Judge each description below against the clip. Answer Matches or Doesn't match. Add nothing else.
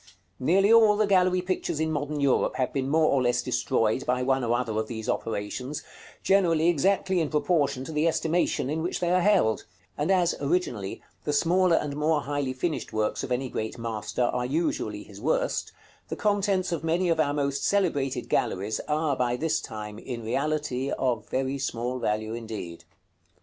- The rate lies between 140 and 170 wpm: Doesn't match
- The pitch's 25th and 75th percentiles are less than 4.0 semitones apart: Doesn't match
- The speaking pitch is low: Doesn't match